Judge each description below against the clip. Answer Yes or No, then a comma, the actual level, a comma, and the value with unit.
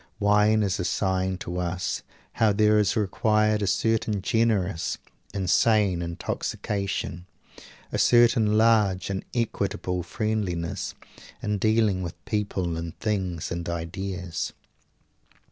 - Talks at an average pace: No, slow, 115 wpm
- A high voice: No, low, 100 Hz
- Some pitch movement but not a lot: Yes, average, 3.0 semitones